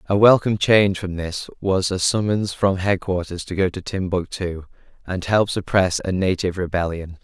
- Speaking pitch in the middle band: No, very low, 95 Hz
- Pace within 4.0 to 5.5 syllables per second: Yes, 5.0 syllables/s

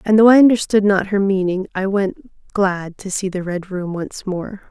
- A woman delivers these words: Yes, female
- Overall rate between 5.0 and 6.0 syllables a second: No, 4.7 syllables/s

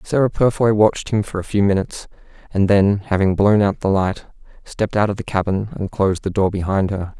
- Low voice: Yes, low, 100 Hz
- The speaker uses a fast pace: Yes, fast, 215 wpm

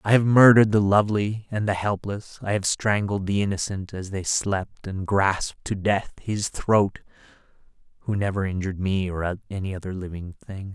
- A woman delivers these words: No, male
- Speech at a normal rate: Yes, average, 175 wpm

